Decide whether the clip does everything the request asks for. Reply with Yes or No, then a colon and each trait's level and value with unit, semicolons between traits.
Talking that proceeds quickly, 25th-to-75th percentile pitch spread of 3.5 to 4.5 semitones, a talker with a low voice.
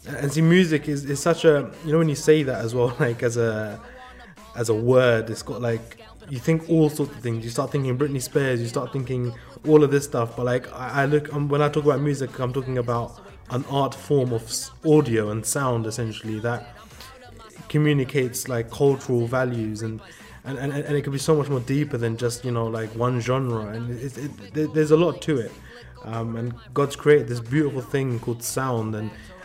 Yes: fast, 215 wpm; average, 3.8 semitones; low, 130 Hz